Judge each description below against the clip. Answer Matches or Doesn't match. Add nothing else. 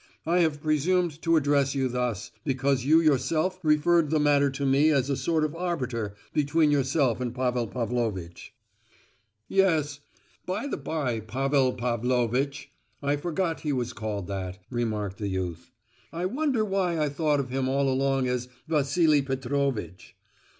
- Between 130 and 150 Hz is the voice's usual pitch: Matches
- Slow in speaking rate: Doesn't match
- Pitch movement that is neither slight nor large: Matches